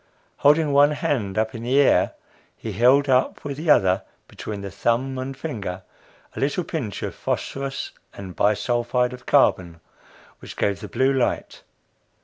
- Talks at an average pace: Yes, average, 160 wpm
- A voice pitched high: No, low, 125 Hz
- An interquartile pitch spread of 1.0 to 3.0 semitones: No, average, 5.1 semitones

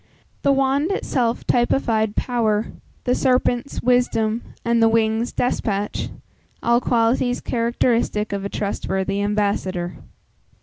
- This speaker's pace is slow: Yes, slow, 105 wpm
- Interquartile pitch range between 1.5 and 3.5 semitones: Yes, average, 2.9 semitones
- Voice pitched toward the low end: No, high, 230 Hz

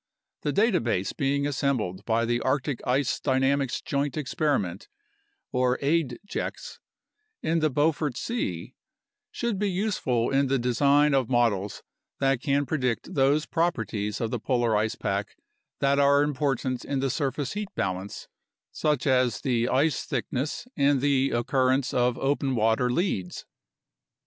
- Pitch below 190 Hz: Yes, low, 135 Hz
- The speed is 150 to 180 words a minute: No, slow, 135 wpm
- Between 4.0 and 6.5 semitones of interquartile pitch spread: No, average, 3.2 semitones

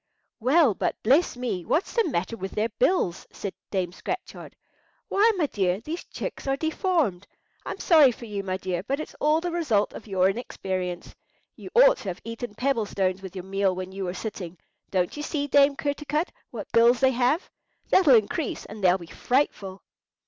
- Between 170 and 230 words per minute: Yes, average, 185 wpm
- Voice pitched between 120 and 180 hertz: No, high, 230 Hz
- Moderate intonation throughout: No, wide, 7.5 semitones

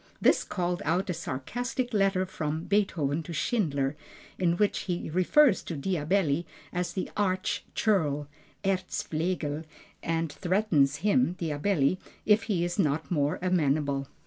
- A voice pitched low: No, medium, 175 Hz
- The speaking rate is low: Yes, slow, 130 wpm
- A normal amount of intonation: Yes, average, 4.4 semitones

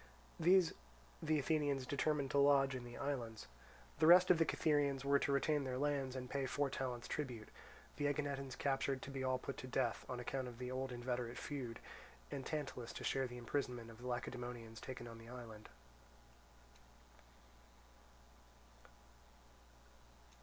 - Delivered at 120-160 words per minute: Yes, average, 155 wpm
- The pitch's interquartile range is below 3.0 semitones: Yes, narrow, 2.6 semitones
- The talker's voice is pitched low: Yes, low, 130 Hz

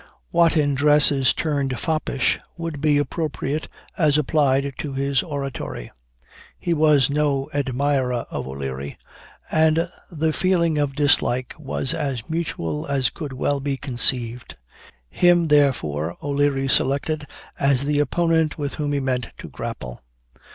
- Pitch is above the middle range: No, medium, 140 Hz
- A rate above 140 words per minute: No, slow, 135 wpm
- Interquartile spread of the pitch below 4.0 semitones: Yes, narrow, 2.6 semitones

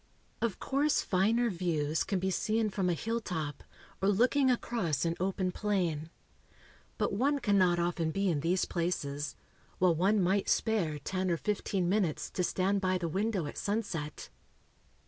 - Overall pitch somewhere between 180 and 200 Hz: Yes, medium, 185 Hz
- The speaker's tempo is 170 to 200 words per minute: No, average, 155 wpm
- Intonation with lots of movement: No, average, 3.8 semitones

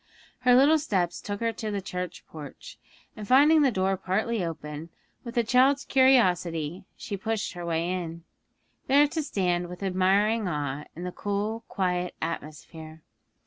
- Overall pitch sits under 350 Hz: Yes, high, 190 Hz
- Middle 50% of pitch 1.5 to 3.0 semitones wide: No, average, 5.2 semitones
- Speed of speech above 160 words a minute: No, average, 155 wpm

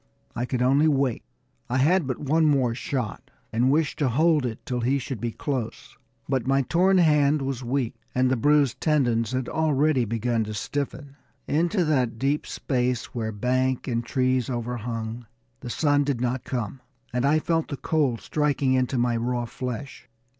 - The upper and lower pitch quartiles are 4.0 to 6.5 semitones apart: No, average, 3.1 semitones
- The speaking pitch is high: No, low, 130 Hz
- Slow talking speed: No, average, 175 wpm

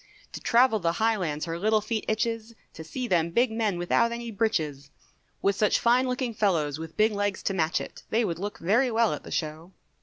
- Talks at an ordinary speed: No, fast, 210 wpm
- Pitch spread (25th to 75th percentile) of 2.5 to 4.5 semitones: No, average, 5.3 semitones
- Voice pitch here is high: Yes, high, 210 Hz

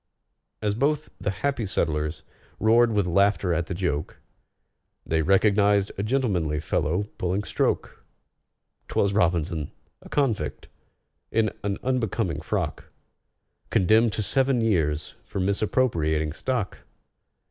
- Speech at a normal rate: No, slow, 110 wpm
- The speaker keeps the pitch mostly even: No, average, 5.1 semitones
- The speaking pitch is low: Yes, low, 100 Hz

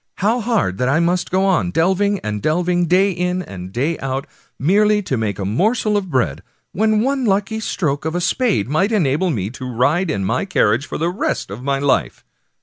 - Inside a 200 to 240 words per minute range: Yes, fast, 205 wpm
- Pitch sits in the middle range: Yes, medium, 175 Hz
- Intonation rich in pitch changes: Yes, wide, 7.1 semitones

